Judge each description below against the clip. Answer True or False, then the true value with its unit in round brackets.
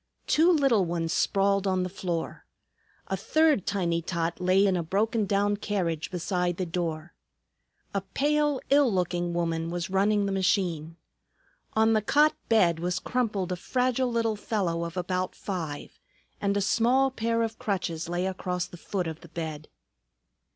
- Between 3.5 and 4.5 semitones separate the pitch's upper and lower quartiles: True (4.1 semitones)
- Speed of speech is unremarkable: True (160 wpm)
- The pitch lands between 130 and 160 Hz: False (190 Hz)